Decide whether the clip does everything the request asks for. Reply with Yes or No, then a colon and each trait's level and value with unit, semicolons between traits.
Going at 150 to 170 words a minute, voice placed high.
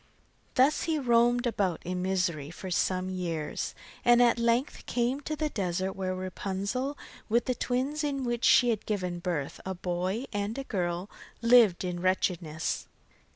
Yes: average, 155 wpm; high, 200 Hz